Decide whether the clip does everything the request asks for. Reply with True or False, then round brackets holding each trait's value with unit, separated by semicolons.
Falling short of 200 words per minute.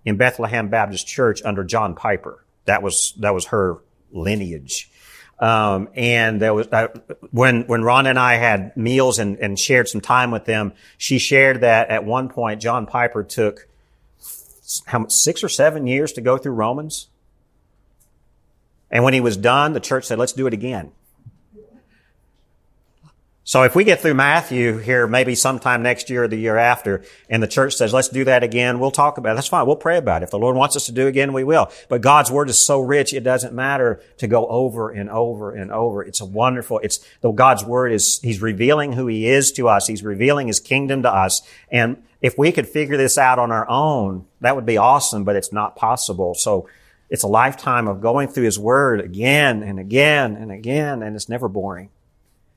False (205 wpm)